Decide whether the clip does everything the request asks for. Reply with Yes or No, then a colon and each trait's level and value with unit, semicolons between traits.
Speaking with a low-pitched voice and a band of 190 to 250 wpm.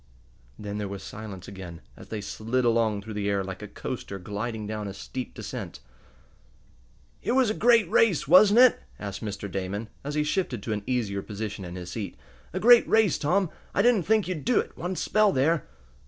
Yes: low, 110 Hz; average, 200 wpm